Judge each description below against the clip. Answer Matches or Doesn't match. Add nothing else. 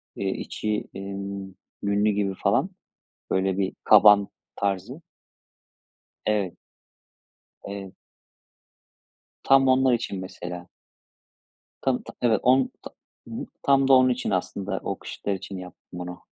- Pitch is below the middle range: Matches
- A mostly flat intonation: Doesn't match